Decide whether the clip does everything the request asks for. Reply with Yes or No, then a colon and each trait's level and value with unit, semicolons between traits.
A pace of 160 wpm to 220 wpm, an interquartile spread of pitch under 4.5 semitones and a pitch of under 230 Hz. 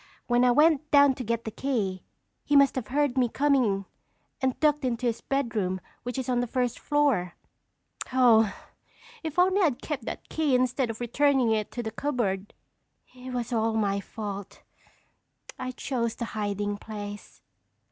No: average, 165 wpm; average, 3.9 semitones; high, 245 Hz